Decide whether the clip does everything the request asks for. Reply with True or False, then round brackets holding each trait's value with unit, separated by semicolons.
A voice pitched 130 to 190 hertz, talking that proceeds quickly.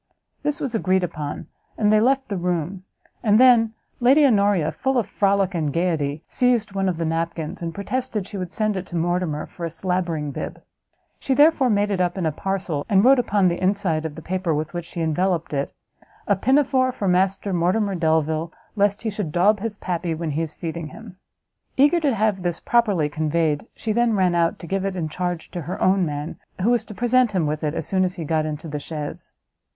True (185 Hz; 215 wpm)